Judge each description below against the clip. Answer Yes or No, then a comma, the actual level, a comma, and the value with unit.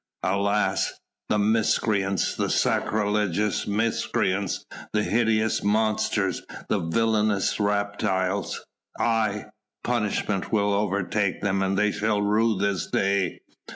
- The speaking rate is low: Yes, slow, 95 wpm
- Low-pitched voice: Yes, low, 105 Hz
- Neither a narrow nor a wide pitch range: No, narrow, 1.6 semitones